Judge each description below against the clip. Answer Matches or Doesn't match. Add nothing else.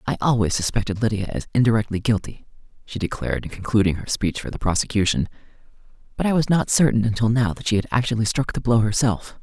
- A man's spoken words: Matches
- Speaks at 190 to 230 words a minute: Matches